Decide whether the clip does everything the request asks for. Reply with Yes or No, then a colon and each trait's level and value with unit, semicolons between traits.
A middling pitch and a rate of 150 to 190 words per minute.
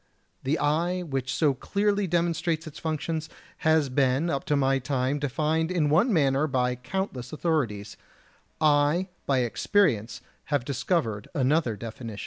No: medium, 145 Hz; slow, 135 wpm